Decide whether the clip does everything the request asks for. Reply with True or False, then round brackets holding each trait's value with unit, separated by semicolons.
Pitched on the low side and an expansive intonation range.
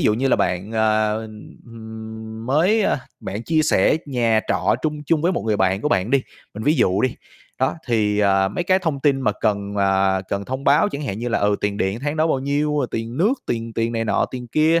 True (115 Hz; 5.7 semitones)